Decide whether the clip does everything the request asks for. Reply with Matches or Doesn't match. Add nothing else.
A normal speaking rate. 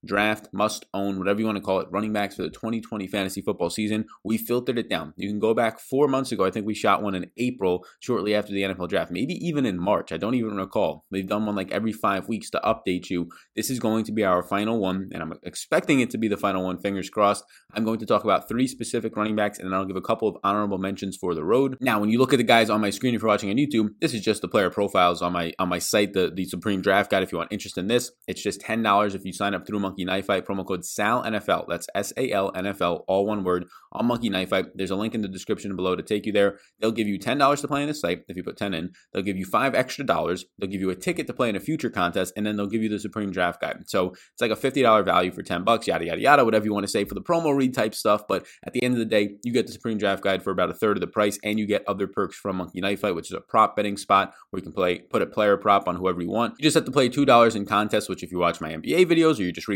Doesn't match